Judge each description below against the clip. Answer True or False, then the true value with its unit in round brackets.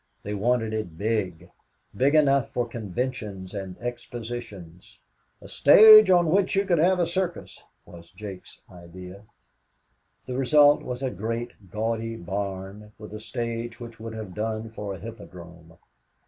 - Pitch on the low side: True (110 Hz)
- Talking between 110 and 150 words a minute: True (145 wpm)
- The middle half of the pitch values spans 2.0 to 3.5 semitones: False (4.4 semitones)